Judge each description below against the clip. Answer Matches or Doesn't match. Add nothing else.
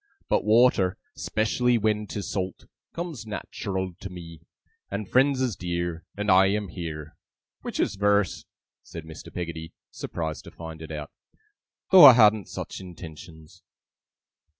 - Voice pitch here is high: Doesn't match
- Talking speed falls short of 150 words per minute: Matches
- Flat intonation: Doesn't match